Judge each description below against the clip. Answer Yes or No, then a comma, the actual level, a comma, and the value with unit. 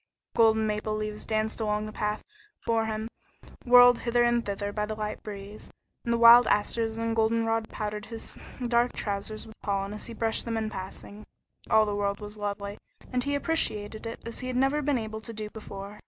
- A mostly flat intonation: Yes, narrow, 1.6 semitones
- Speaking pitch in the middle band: No, high, 220 Hz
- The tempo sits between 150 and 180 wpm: No, average, 200 wpm